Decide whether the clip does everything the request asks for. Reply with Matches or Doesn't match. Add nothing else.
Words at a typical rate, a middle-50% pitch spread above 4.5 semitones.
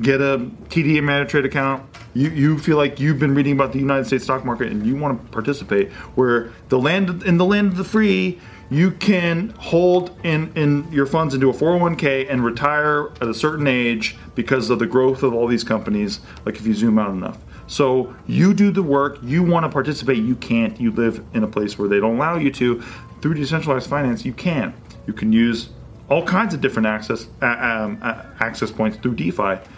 Doesn't match